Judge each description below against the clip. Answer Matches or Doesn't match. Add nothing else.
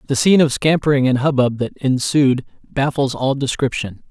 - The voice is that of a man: Matches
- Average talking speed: Matches